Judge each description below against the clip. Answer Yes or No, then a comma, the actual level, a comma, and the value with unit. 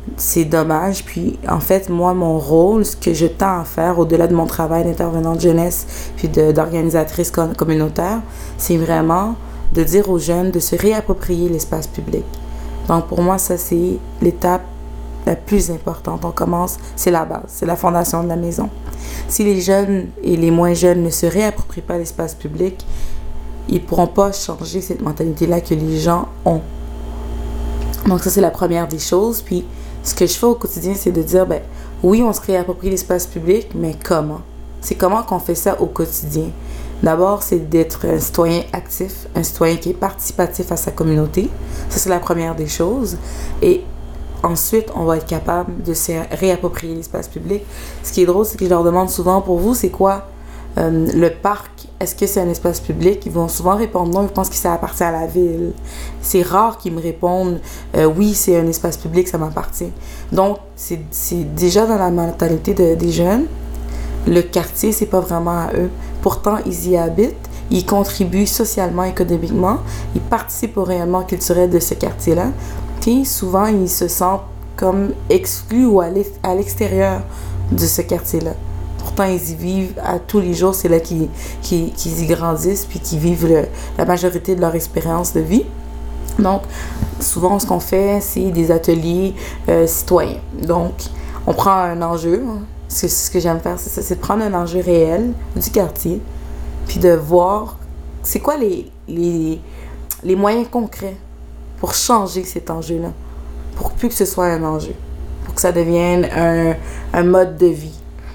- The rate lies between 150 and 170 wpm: No, average, 180 wpm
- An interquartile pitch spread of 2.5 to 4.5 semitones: Yes, average, 2.8 semitones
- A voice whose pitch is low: No, medium, 175 Hz